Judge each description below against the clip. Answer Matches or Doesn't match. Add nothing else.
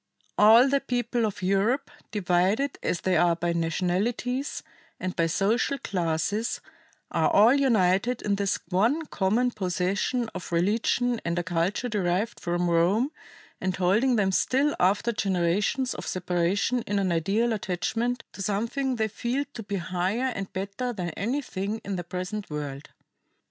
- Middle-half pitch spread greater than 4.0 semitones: Matches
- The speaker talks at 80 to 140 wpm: Doesn't match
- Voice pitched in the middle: Doesn't match